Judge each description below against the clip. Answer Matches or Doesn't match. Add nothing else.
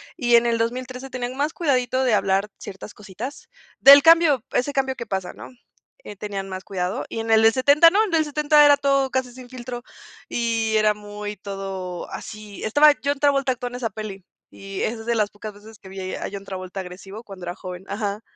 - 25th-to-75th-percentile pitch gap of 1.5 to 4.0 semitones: Doesn't match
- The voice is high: Matches